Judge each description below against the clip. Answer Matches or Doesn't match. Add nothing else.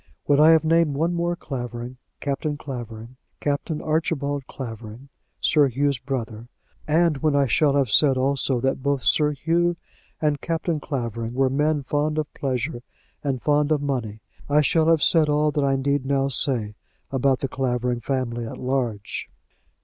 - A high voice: Doesn't match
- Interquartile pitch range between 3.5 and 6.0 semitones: Doesn't match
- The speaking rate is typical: Matches